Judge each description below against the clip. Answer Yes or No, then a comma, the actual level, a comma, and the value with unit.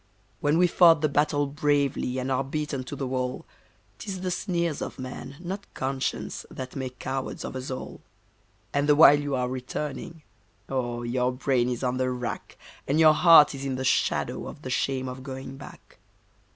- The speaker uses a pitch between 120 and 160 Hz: Yes, low, 135 Hz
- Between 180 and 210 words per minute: Yes, average, 185 wpm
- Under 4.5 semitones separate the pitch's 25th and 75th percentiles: Yes, narrow, 2.6 semitones